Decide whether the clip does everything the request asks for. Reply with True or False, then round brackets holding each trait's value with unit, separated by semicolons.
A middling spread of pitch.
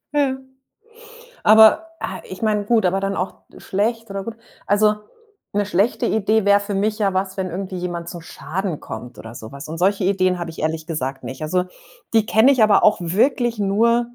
True (3.7 semitones)